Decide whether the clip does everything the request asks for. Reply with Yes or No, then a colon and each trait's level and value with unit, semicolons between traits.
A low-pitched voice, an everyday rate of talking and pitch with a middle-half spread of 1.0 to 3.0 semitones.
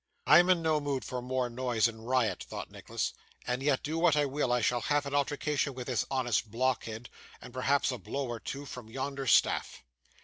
No: low, 130 Hz; fast, 210 wpm; average, 2.7 semitones